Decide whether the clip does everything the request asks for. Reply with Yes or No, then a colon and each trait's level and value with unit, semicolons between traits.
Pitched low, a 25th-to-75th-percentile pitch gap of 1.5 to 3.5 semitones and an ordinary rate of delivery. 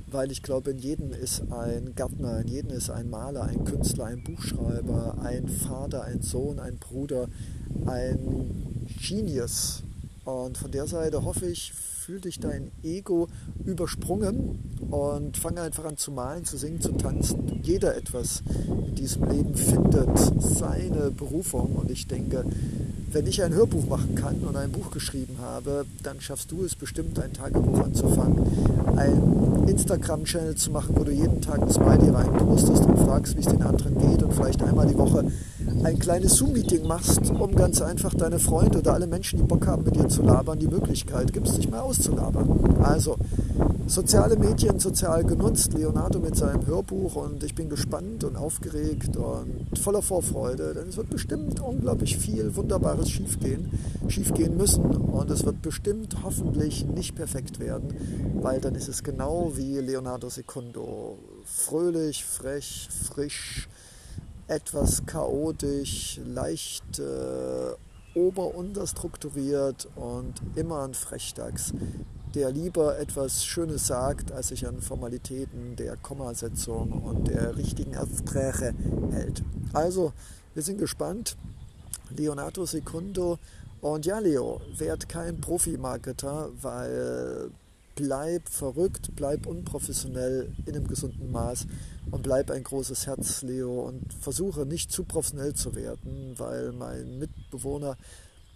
No: low, 130 Hz; average, 5.3 semitones; average, 140 wpm